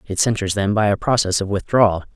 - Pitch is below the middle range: Yes, low, 105 Hz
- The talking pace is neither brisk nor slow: No, fast, 225 wpm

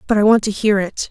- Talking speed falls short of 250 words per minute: No, fast, 325 wpm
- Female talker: Yes, female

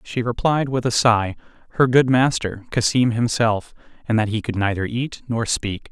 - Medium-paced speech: Yes, average, 180 wpm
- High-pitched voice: No, low, 115 Hz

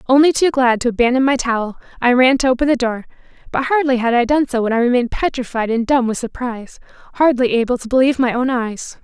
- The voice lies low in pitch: No, very high, 250 Hz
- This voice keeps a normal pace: No, fast, 225 wpm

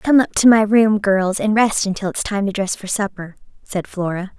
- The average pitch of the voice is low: No, high, 205 Hz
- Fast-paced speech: Yes, fast, 235 wpm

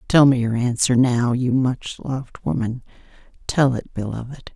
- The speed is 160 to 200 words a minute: No, average, 145 wpm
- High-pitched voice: No, low, 125 Hz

